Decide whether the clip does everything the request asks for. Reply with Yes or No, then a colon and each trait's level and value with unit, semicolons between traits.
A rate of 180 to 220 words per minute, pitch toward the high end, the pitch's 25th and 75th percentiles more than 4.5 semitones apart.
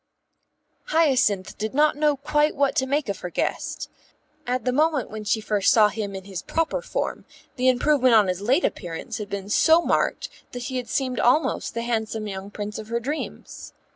Yes: average, 195 wpm; high, 240 Hz; wide, 5.5 semitones